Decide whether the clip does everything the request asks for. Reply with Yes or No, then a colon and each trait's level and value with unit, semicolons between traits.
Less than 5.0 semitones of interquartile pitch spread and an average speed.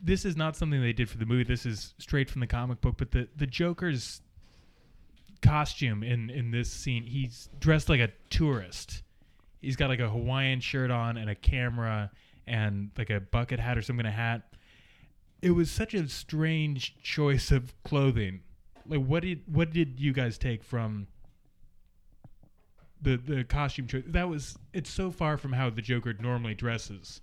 Yes: average, 3.8 semitones; average, 180 wpm